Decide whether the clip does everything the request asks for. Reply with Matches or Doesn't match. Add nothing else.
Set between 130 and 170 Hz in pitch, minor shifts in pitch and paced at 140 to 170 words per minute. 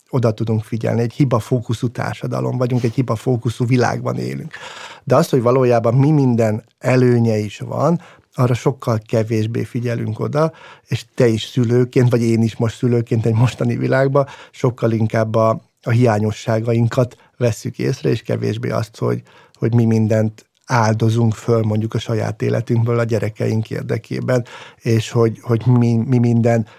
Doesn't match